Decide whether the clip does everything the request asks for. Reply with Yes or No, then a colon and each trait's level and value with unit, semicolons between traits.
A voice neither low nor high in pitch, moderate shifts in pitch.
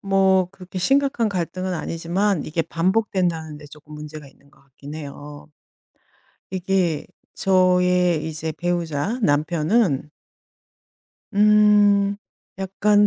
Yes: medium, 180 Hz; average, 4.2 semitones